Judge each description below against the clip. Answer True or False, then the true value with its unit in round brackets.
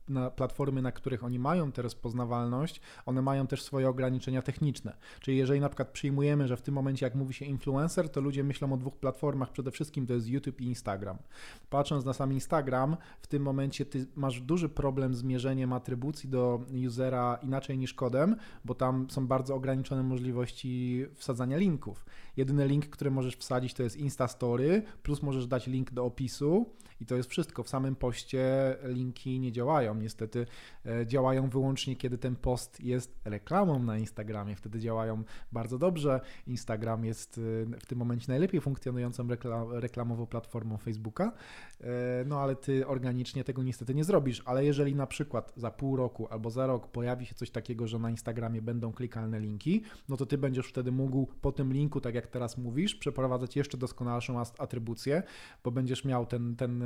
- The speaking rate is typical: False (175 wpm)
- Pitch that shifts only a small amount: True (2.1 semitones)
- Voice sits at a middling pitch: False (130 Hz)